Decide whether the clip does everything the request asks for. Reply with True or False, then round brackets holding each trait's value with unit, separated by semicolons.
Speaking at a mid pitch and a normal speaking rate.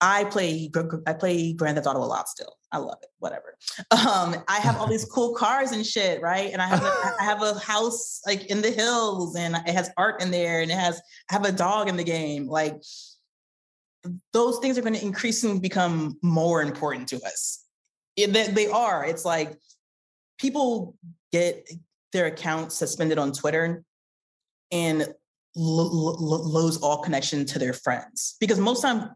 True (175 Hz; 180 wpm)